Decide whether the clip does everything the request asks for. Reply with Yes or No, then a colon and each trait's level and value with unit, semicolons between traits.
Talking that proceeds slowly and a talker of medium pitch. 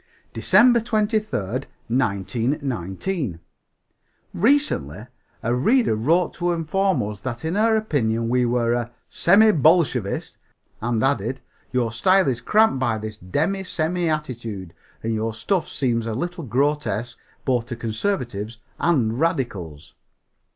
No: slow, 125 wpm; low, 130 Hz